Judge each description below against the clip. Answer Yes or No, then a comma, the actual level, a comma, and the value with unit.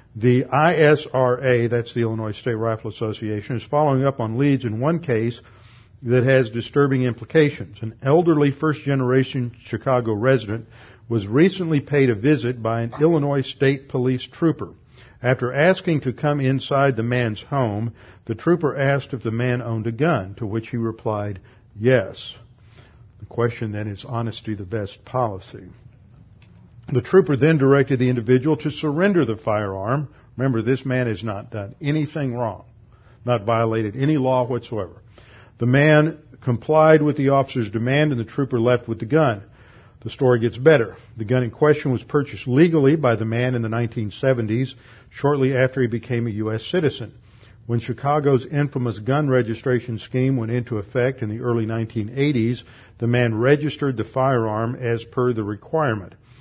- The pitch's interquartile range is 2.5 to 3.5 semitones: Yes, average, 3.2 semitones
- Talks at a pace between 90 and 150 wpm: No, average, 160 wpm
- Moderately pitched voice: No, low, 125 Hz